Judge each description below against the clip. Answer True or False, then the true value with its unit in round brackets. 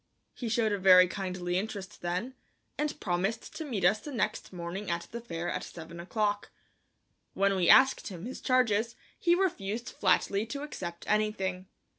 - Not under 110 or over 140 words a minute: False (165 wpm)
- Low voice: False (205 Hz)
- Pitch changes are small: False (4.2 semitones)